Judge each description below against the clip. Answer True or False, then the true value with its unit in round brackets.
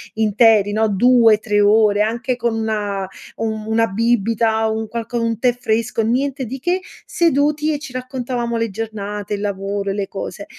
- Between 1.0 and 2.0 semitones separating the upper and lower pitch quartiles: False (2.7 semitones)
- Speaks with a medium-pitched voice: False (225 Hz)